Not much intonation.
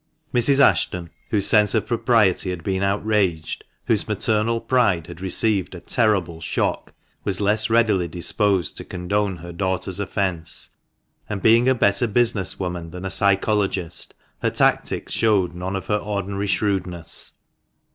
No: average, 3.0 semitones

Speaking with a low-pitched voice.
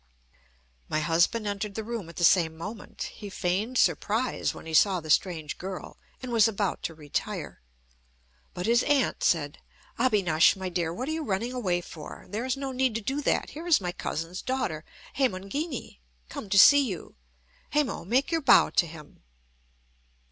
No: high, 200 Hz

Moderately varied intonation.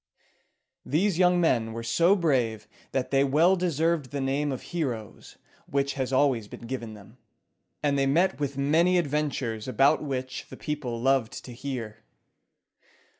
Yes: average, 3.9 semitones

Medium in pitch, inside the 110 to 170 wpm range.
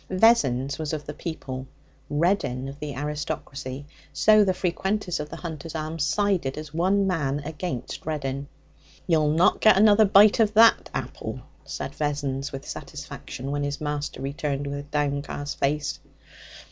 Yes: medium, 150 Hz; average, 145 wpm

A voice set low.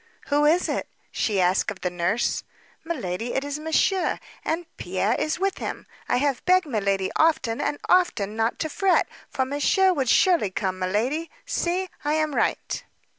No: very high, 285 Hz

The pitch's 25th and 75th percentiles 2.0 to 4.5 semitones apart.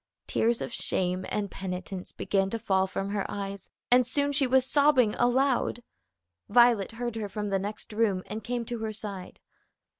Yes: average, 3.7 semitones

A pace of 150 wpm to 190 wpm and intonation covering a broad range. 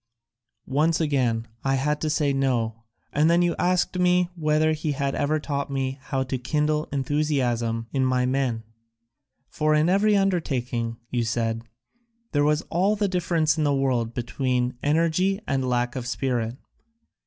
No: average, 155 wpm; average, 3.8 semitones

